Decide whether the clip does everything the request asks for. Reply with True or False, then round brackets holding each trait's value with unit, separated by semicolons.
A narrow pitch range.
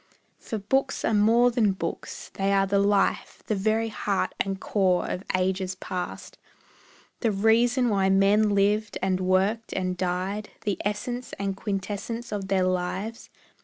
True (2.3 semitones)